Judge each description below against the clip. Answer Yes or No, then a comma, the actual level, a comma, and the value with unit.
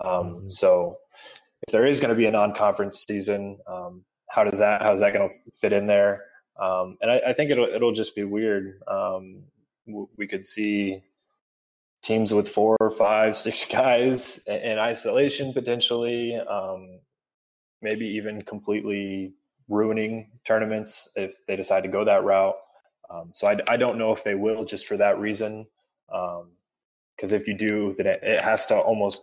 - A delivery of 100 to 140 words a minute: No, average, 170 wpm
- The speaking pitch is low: Yes, low, 105 Hz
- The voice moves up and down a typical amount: No, narrow, 2.3 semitones